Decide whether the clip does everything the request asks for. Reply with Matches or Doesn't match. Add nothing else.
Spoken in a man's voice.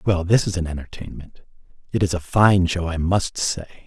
Matches